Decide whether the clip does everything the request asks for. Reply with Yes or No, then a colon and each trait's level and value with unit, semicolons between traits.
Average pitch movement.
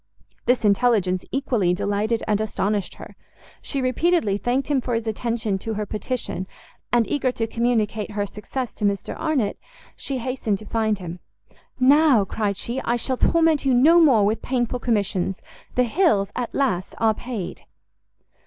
Yes: average, 3.8 semitones